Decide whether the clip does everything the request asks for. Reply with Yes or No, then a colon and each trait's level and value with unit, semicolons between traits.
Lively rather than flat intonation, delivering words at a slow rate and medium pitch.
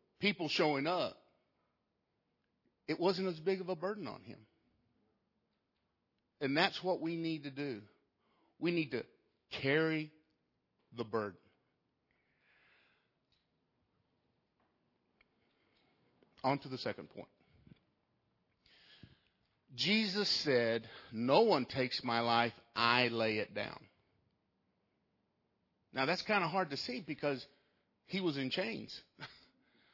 Yes: wide, 7.1 semitones; slow, 105 wpm; medium, 145 Hz